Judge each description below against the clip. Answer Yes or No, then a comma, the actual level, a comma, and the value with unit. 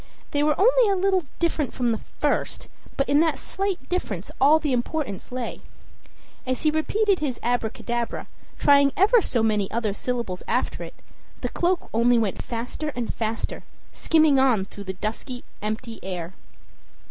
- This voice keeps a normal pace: Yes, average, 160 wpm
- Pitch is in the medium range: No, very high, 255 Hz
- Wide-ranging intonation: Yes, wide, 5.9 semitones